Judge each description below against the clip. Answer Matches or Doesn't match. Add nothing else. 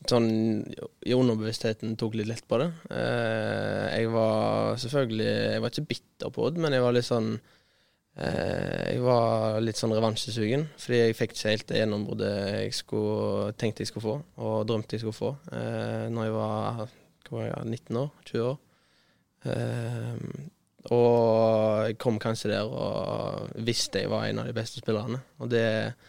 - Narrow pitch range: Matches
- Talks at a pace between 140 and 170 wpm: Matches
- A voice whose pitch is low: Matches